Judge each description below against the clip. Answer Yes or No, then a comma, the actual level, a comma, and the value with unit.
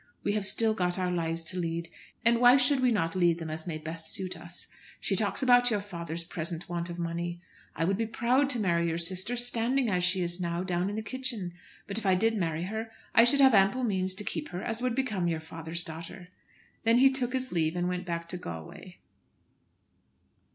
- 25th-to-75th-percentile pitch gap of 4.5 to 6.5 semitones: Yes, average, 5.1 semitones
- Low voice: No, medium, 185 Hz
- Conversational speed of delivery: No, fast, 220 wpm